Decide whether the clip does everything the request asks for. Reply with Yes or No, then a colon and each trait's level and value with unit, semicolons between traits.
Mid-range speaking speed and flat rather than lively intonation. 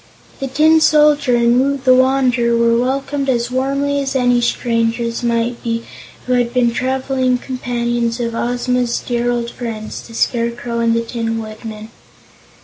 Yes: average, 155 wpm; narrow, 1.9 semitones